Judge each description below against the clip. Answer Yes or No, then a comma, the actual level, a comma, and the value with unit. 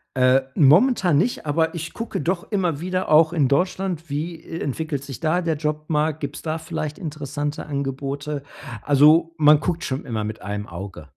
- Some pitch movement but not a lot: Yes, average, 3.0 semitones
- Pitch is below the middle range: No, medium, 150 Hz